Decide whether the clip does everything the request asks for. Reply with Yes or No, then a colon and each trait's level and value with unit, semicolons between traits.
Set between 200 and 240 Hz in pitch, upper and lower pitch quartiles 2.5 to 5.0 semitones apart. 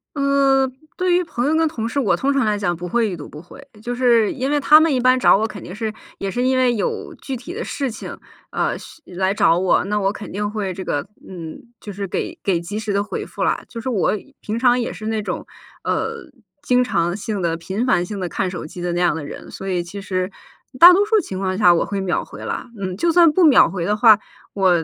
No: high, 210 Hz; wide, 5.6 semitones